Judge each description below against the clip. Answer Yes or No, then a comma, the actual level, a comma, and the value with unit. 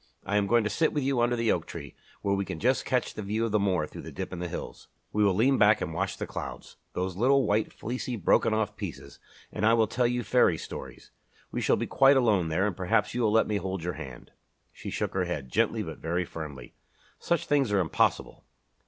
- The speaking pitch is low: Yes, low, 105 Hz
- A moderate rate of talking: No, fast, 240 wpm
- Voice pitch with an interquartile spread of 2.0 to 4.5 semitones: No, average, 4.9 semitones